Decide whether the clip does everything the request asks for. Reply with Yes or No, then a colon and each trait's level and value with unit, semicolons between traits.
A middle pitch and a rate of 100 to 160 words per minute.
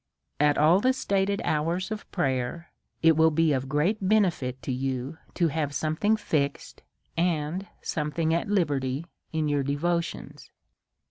Yes: medium, 160 Hz; average, 145 wpm